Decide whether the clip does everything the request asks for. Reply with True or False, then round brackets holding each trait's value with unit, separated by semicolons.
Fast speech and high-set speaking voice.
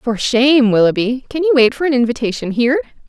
False (195 wpm; 250 Hz)